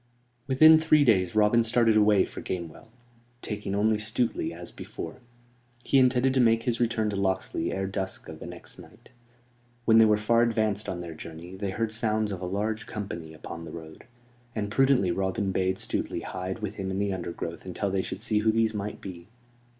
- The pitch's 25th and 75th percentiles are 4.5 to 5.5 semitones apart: No, average, 3.2 semitones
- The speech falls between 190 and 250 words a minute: Yes, average, 195 wpm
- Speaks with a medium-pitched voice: No, low, 105 Hz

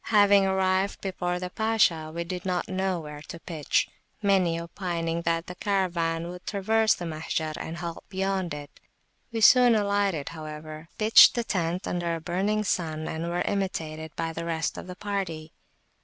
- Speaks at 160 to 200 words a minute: Yes, average, 170 wpm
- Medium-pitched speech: Yes, medium, 175 Hz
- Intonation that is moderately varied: Yes, average, 3.1 semitones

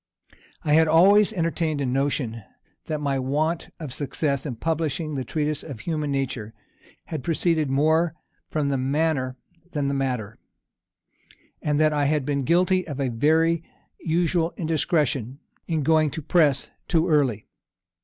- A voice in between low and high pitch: Yes, medium, 150 Hz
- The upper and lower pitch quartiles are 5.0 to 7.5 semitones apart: No, average, 3.0 semitones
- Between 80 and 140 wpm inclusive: No, average, 150 wpm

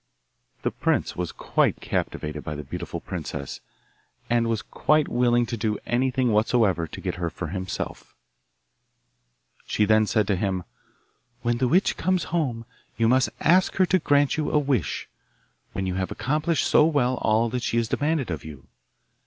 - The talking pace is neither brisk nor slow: Yes, average, 170 wpm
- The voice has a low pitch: Yes, low, 115 Hz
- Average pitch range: No, wide, 6.7 semitones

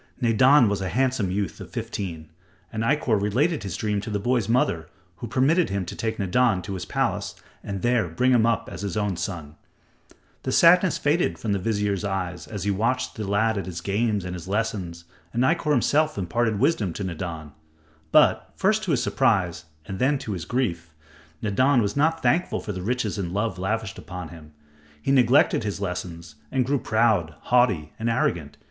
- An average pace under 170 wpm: No, average, 190 wpm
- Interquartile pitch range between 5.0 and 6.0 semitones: Yes, average, 5.3 semitones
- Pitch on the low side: Yes, low, 105 Hz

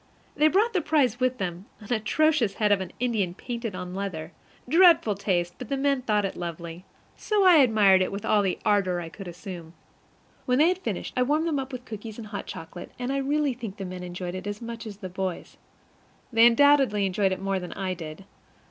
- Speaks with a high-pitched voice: Yes, high, 210 Hz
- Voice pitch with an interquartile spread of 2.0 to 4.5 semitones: No, wide, 5.6 semitones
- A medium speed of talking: No, fast, 220 wpm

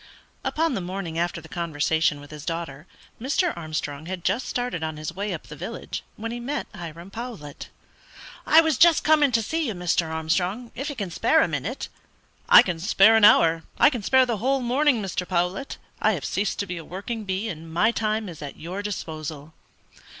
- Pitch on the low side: No, high, 190 Hz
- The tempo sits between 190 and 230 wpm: Yes, average, 200 wpm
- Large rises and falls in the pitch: Yes, wide, 6.5 semitones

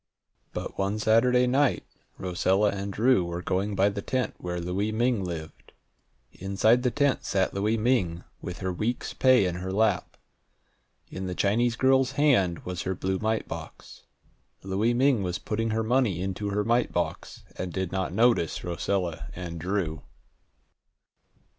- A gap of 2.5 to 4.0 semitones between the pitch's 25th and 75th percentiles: No, average, 4.4 semitones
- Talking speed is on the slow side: No, average, 155 wpm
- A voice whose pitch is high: No, low, 100 Hz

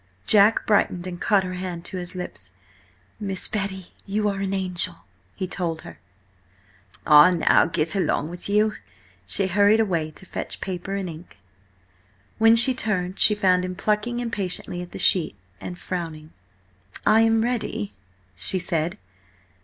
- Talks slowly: No, average, 155 wpm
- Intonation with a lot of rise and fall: No, average, 3.0 semitones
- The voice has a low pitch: No, medium, 185 Hz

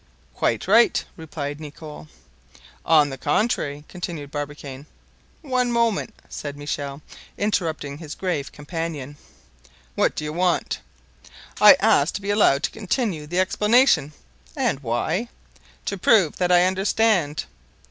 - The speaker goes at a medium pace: No, slow, 125 wpm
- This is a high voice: No, medium, 160 Hz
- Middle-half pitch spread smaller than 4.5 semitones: No, average, 5.3 semitones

